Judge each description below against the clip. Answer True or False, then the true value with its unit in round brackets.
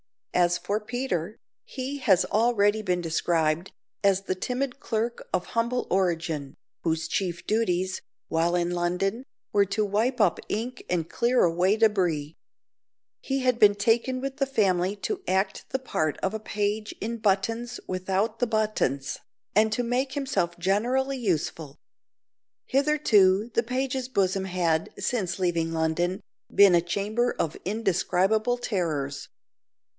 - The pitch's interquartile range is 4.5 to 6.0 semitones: True (5.1 semitones)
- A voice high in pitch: True (200 Hz)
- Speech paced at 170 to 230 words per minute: False (140 wpm)